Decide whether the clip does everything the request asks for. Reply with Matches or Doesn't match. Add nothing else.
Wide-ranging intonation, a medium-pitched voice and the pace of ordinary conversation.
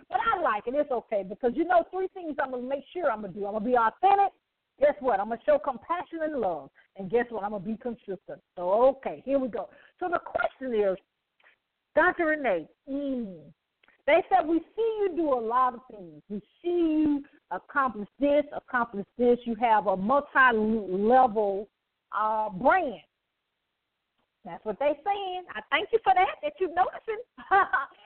Doesn't match